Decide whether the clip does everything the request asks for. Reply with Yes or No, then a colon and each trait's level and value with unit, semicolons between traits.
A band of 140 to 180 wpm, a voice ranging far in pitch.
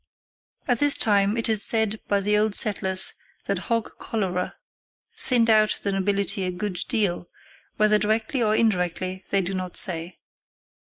No: average, 155 wpm; average, 2.8 semitones